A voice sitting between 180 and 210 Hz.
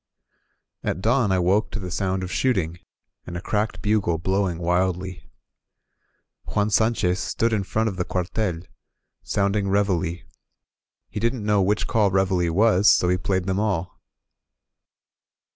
No: very low, 95 Hz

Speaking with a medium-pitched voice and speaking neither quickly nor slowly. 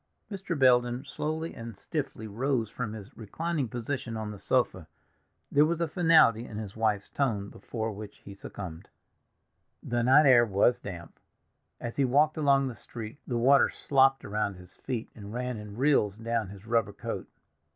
No: low, 120 Hz; average, 170 wpm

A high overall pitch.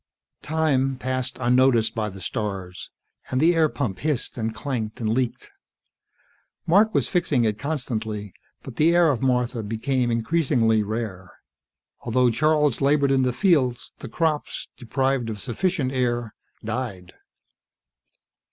No: low, 125 Hz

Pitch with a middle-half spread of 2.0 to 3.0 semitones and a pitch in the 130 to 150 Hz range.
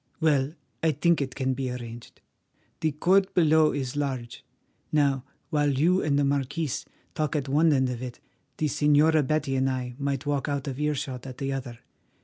Yes: narrow, 2.6 semitones; medium, 140 Hz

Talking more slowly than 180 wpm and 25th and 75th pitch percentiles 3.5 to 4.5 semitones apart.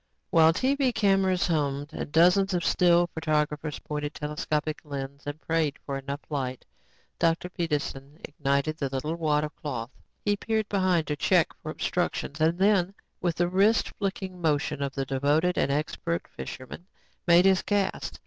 Yes: average, 160 wpm; average, 3.8 semitones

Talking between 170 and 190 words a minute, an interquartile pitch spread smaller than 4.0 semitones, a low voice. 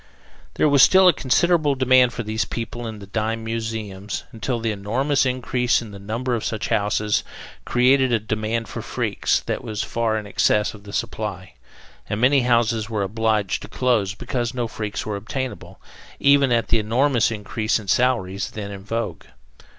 Yes: average, 175 wpm; average, 2.9 semitones; low, 115 Hz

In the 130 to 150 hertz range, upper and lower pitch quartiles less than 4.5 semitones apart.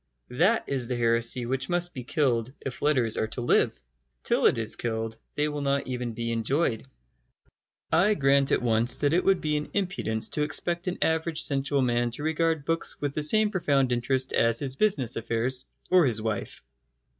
No: low, 135 Hz; average, 4.9 semitones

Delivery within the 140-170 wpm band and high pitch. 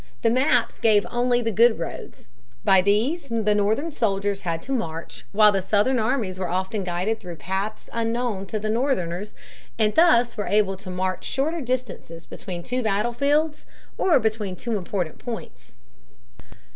Yes: average, 160 wpm; high, 215 Hz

